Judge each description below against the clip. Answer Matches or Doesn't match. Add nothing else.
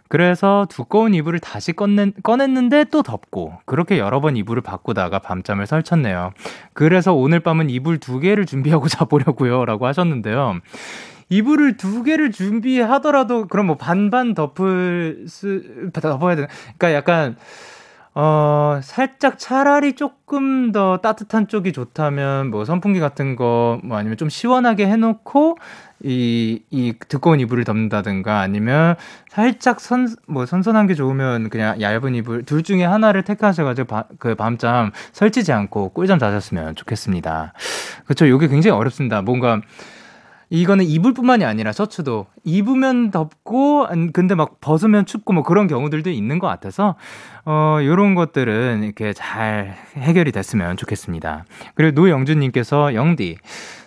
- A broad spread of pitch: Matches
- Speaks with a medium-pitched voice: Matches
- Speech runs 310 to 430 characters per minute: Matches